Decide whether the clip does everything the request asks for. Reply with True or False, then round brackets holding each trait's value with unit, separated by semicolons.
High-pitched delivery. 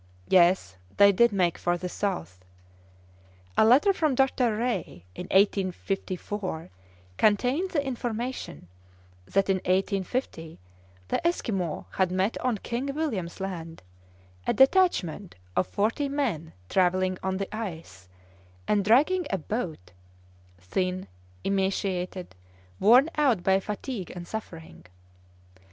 True (195 Hz)